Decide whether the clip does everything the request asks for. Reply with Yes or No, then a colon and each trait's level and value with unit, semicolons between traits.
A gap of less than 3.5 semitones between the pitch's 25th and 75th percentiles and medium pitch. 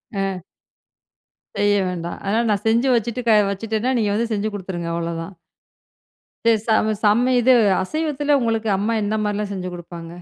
No: average, 3.0 semitones; high, 210 Hz